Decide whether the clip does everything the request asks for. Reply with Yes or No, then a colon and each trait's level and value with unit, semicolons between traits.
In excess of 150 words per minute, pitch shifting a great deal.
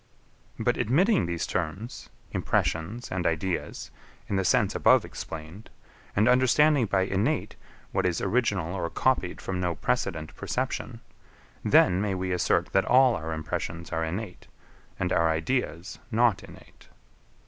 No: slow, 135 wpm; wide, 5.8 semitones